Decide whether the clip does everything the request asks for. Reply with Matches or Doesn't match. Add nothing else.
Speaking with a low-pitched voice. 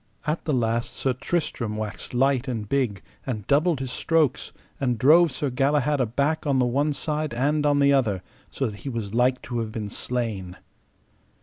Matches